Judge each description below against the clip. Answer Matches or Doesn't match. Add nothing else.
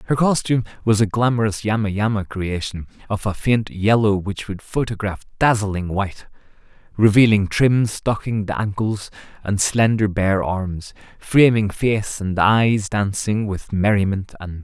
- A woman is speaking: Doesn't match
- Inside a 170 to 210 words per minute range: Doesn't match